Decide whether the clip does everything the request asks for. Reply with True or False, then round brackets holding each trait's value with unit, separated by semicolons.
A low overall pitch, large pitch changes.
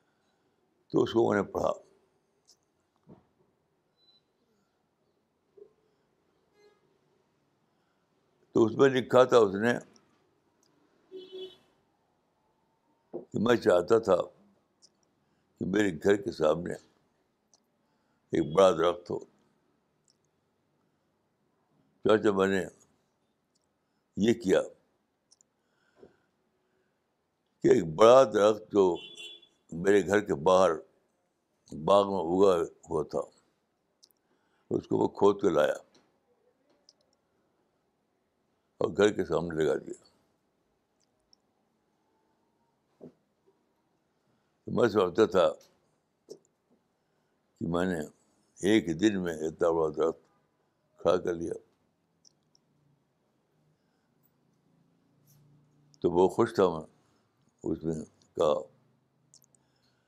True (110 Hz; 7.7 semitones)